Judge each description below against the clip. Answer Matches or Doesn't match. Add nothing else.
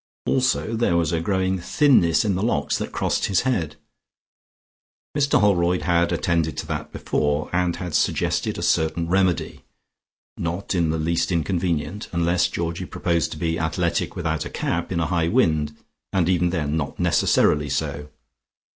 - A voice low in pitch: Matches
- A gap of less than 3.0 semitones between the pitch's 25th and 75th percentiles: Matches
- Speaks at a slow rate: Doesn't match